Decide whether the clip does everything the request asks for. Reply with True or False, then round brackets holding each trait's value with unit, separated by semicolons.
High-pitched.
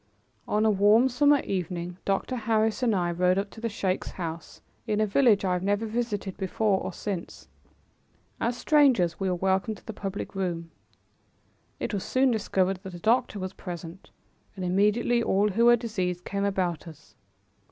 True (200 Hz)